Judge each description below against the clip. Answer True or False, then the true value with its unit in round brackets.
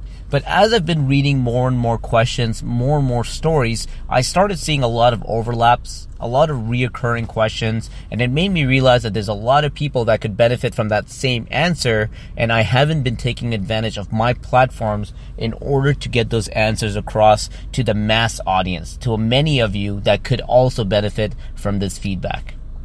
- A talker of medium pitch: False (115 Hz)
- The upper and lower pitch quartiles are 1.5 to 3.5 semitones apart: True (2.8 semitones)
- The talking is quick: False (195 wpm)